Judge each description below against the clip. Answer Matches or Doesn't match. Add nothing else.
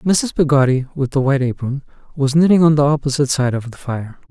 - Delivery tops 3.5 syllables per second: Matches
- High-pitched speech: Doesn't match